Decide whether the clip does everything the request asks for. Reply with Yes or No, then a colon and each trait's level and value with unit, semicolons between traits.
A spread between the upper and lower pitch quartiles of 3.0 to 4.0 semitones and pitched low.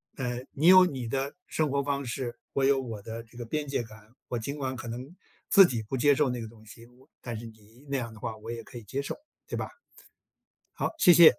Yes: average, 3.4 semitones; low, 125 Hz